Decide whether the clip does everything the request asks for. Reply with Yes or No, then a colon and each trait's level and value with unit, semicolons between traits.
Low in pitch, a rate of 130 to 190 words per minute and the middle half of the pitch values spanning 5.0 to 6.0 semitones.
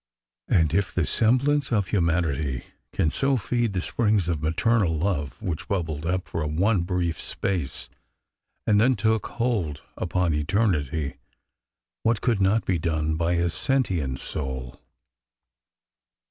Yes: very low, 90 Hz; slow, 135 wpm; wide, 5.5 semitones